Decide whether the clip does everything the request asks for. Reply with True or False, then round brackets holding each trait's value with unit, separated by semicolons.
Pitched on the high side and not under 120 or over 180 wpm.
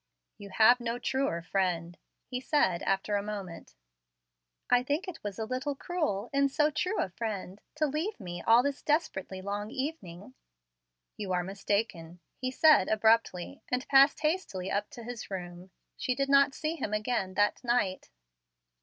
True (225 Hz; 165 wpm)